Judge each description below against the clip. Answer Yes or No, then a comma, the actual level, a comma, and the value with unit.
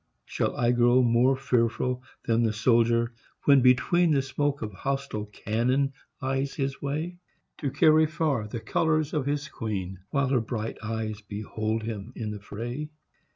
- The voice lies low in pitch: Yes, low, 125 Hz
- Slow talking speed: No, average, 155 wpm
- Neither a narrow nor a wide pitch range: Yes, average, 3.9 semitones